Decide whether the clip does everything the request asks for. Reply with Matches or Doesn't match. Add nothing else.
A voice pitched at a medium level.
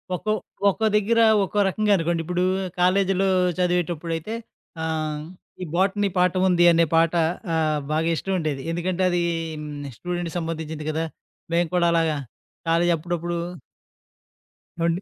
Matches